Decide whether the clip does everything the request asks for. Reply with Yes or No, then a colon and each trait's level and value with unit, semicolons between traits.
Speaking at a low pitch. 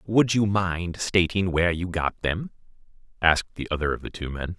Yes: very low, 90 Hz